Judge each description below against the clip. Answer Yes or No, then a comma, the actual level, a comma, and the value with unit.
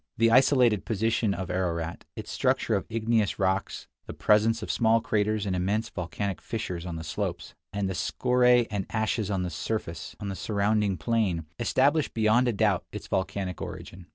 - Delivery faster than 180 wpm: No, average, 160 wpm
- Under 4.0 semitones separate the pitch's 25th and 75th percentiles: Yes, average, 3.5 semitones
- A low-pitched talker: Yes, low, 105 Hz